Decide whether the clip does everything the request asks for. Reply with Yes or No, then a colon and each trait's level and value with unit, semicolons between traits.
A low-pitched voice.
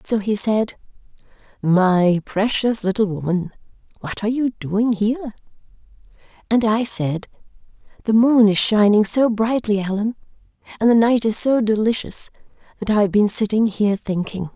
No: high, 210 Hz